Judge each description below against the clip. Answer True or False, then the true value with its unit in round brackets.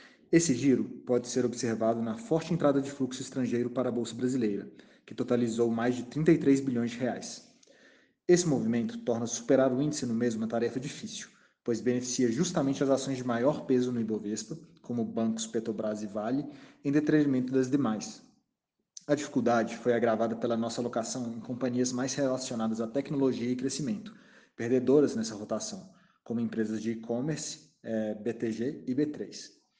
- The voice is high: False (125 Hz)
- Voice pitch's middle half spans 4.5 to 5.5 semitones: False (4.0 semitones)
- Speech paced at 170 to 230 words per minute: False (160 wpm)